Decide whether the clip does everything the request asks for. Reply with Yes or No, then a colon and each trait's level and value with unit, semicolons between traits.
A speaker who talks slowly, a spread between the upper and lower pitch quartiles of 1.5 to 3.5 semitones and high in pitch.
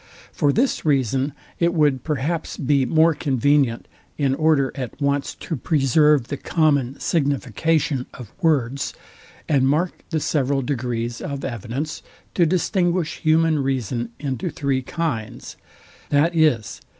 No: slow, 125 wpm; average, 3.2 semitones; medium, 140 Hz